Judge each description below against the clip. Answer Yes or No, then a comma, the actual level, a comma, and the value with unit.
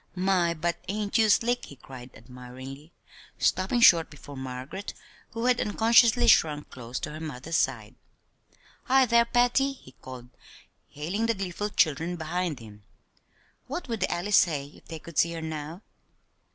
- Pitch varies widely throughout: Yes, wide, 7.2 semitones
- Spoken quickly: No, average, 155 wpm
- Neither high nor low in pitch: Yes, medium, 170 Hz